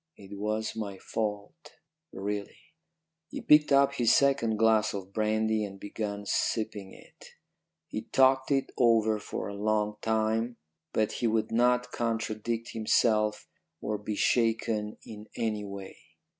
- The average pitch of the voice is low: Yes, low, 110 Hz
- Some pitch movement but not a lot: No, narrow, 1.7 semitones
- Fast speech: No, slow, 135 wpm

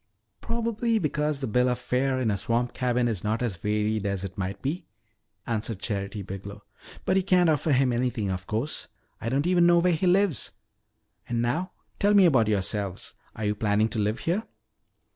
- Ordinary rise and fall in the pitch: No, wide, 7.4 semitones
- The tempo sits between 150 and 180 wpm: No, average, 190 wpm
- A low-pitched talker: Yes, low, 120 Hz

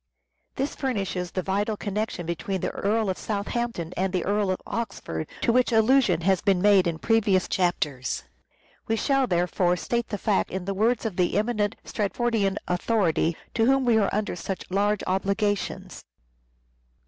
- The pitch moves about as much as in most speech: Yes, average, 3.7 semitones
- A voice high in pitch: Yes, high, 200 Hz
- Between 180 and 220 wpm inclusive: No, average, 160 wpm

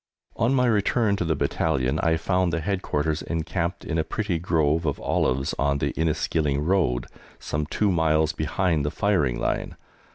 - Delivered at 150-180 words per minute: Yes, average, 165 wpm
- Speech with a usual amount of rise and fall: Yes, average, 3.8 semitones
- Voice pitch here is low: Yes, very low, 80 Hz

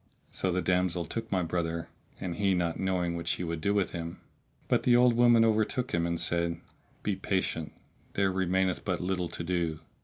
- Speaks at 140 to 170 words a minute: No, average, 190 wpm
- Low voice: Yes, very low, 90 Hz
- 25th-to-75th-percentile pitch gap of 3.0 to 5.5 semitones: No, narrow, 2.4 semitones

